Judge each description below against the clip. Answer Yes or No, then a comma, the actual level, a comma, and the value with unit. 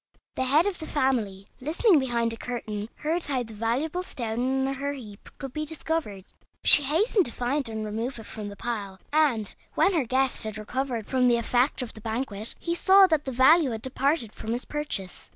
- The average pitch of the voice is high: Yes, very high, 255 Hz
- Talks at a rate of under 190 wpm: No, fast, 205 wpm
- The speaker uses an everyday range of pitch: Yes, average, 5.0 semitones